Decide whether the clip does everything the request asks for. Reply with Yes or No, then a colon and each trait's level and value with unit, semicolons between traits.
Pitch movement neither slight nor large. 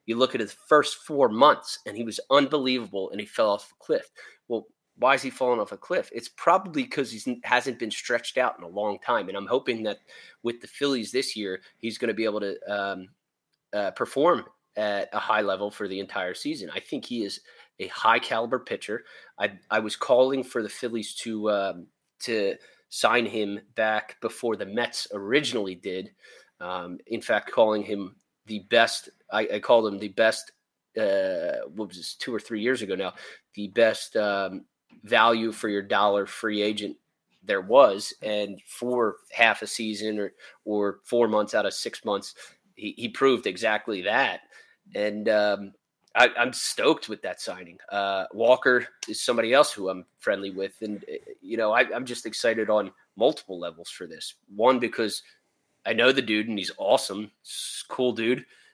Yes: average, 3.3 semitones